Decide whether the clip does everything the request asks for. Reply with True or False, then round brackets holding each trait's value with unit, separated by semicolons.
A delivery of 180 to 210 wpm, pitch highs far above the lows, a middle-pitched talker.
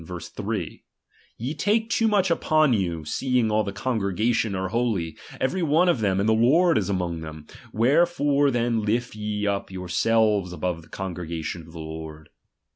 False (190 wpm; 6.6 semitones; 105 Hz)